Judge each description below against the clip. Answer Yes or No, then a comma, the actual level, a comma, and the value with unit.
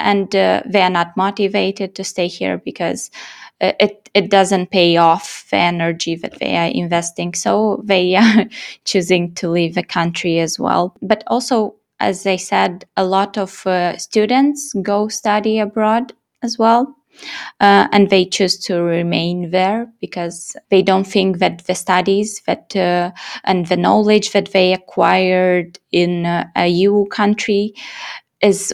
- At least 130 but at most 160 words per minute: Yes, average, 155 wpm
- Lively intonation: No, average, 2.8 semitones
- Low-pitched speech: No, high, 190 Hz